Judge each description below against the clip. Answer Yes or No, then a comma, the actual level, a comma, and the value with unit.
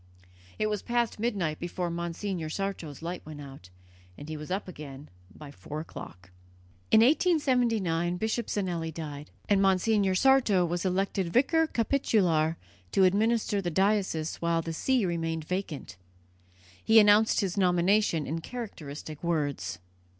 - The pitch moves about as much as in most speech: Yes, average, 4.9 semitones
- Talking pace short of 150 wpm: Yes, slow, 135 wpm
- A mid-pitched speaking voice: Yes, medium, 180 Hz